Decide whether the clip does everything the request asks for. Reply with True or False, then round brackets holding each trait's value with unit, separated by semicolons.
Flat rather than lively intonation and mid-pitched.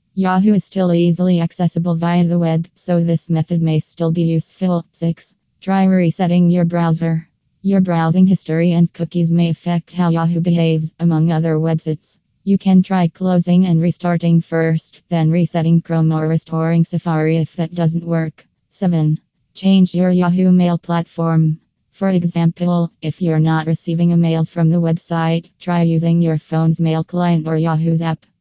True (1.3 semitones; 170 Hz)